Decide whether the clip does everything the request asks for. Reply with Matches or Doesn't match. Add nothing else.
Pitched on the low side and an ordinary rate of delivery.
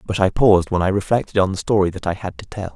Doesn't match